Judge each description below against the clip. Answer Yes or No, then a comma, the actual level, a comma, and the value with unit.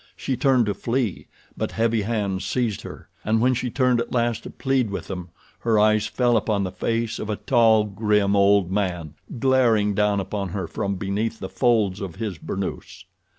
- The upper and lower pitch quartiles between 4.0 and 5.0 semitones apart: No, average, 2.9 semitones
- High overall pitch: No, low, 105 Hz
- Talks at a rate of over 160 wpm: Yes, average, 190 wpm